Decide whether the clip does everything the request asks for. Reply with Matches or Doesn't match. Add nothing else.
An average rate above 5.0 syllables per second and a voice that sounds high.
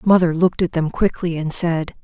Doesn't match